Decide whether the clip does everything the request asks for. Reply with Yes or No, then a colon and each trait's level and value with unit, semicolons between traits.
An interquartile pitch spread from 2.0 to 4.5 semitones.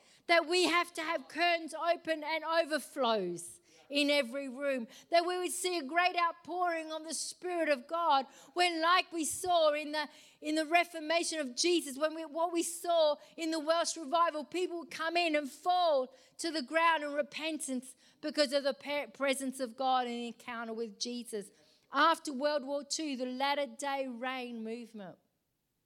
Yes: average, 3.8 semitones